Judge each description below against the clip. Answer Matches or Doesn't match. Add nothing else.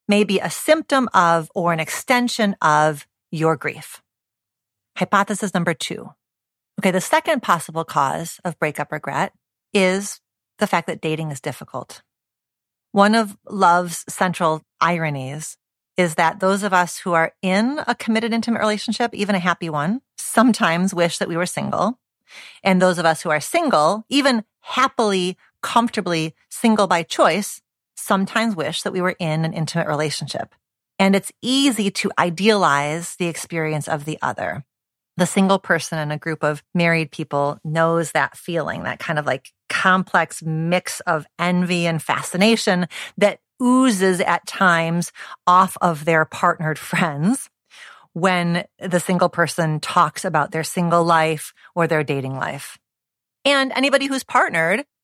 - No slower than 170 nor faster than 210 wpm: Doesn't match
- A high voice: Doesn't match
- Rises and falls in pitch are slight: Doesn't match